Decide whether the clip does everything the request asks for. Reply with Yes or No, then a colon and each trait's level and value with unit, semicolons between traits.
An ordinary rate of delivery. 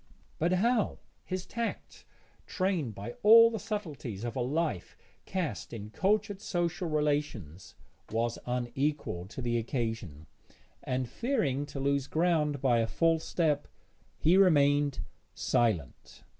No: slow, 125 wpm